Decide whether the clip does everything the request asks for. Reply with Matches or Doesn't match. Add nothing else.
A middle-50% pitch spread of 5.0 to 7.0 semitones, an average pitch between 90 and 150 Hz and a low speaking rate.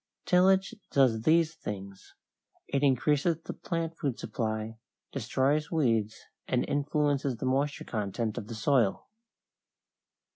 Matches